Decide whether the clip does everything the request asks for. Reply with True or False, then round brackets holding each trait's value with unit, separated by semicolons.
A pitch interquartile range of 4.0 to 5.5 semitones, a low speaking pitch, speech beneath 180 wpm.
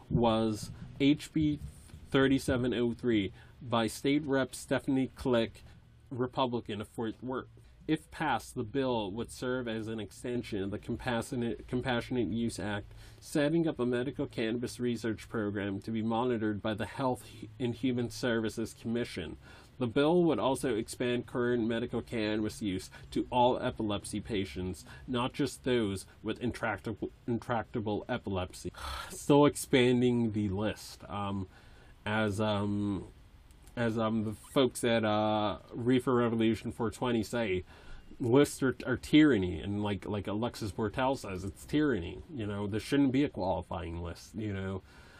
False (3.2 semitones; 115 Hz; 140 wpm)